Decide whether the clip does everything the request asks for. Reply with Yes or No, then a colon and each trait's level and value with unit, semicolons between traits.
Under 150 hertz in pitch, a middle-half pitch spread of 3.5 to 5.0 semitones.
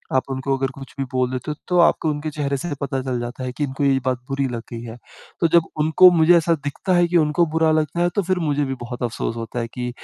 Yes: medium, 140 Hz; average, 3.8 semitones